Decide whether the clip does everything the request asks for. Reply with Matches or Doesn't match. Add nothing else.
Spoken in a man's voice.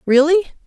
Doesn't match